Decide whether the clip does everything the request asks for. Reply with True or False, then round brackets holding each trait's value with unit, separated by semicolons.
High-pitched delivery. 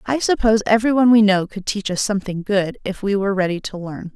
True (205 Hz)